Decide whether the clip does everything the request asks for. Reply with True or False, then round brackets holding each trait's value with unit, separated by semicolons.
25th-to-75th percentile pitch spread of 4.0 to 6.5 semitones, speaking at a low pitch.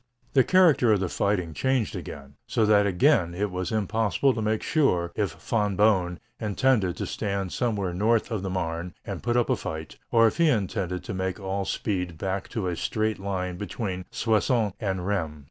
False (3.5 semitones; 100 Hz)